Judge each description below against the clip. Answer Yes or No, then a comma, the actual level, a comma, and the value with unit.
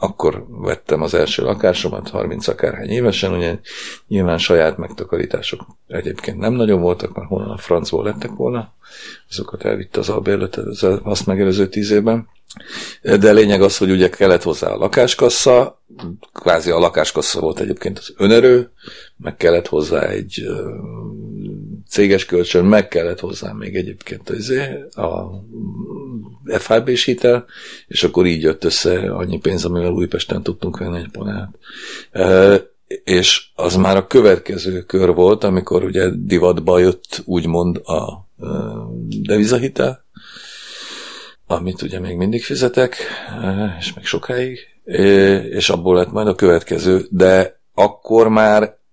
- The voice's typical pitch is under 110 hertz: Yes, very low, 95 Hz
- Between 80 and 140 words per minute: Yes, average, 130 wpm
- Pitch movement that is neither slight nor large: Yes, average, 3.3 semitones